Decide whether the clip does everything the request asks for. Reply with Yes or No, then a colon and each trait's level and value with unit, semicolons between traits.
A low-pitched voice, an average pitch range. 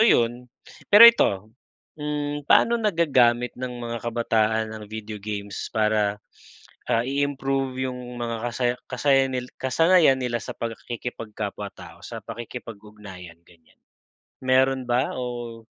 Yes: low, 120 Hz; average, 3.3 semitones